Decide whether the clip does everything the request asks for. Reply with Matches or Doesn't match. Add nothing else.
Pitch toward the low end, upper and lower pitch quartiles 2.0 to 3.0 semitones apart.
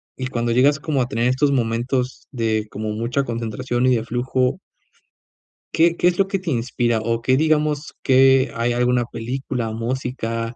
Matches